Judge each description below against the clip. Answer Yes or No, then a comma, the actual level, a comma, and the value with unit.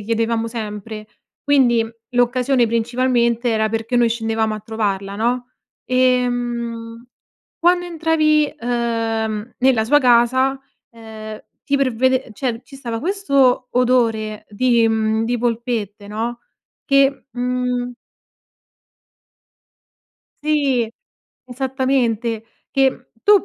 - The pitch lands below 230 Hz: No, high, 240 Hz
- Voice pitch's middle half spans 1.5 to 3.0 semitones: Yes, narrow, 2.5 semitones